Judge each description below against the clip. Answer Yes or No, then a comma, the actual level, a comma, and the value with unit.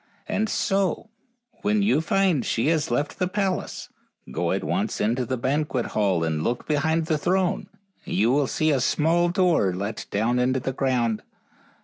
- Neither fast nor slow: Yes, average, 170 wpm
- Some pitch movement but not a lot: No, wide, 6.5 semitones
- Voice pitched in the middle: Yes, medium, 145 Hz